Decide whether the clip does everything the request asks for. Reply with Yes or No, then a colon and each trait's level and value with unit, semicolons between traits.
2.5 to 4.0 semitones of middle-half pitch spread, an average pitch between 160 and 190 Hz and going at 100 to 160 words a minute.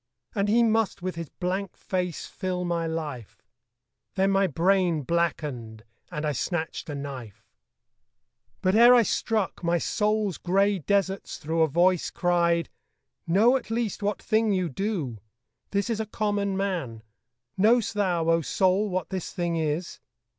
Yes: average, 3.6 semitones; medium, 185 Hz; average, 150 wpm